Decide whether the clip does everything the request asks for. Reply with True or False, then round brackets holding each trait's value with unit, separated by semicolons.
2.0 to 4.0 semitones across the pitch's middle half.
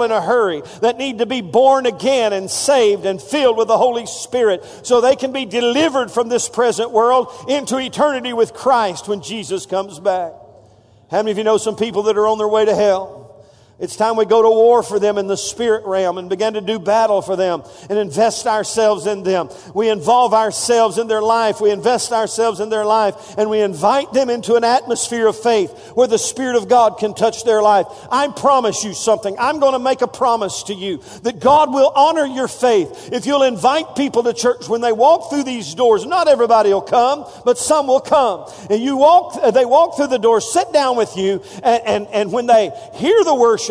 True (3.5 semitones)